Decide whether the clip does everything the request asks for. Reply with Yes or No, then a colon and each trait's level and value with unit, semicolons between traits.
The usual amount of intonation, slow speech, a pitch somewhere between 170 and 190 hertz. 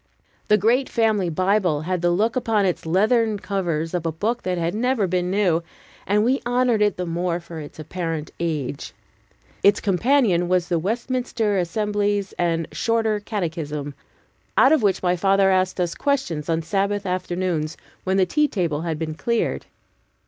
No: average, 4.1 semitones; average, 165 wpm; medium, 185 Hz